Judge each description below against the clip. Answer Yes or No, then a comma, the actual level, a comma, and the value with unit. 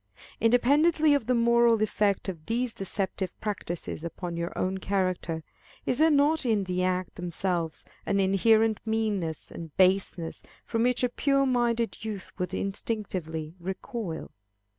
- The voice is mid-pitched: No, high, 200 Hz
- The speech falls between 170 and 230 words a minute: No, average, 140 wpm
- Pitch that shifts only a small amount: No, average, 4.5 semitones